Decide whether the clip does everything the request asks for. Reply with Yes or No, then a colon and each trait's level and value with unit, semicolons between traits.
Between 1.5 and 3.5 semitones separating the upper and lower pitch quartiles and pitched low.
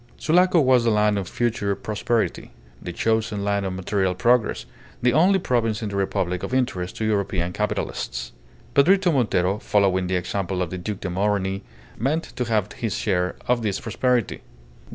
No: average, 4.2 semitones; low, 105 Hz